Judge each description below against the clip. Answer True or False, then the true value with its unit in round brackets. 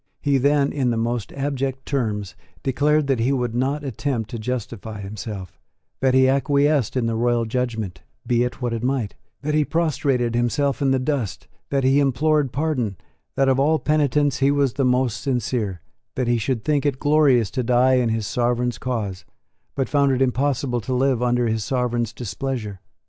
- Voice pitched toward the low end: True (125 Hz)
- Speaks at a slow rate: False (180 wpm)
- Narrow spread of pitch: False (3.0 semitones)